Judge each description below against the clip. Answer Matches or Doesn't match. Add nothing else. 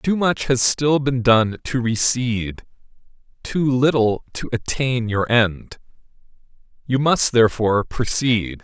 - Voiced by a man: Matches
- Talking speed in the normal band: Doesn't match